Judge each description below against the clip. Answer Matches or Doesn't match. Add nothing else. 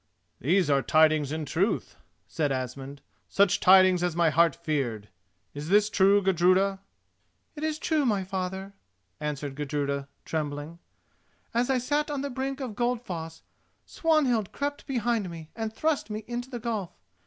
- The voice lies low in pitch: Doesn't match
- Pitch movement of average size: Doesn't match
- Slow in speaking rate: Doesn't match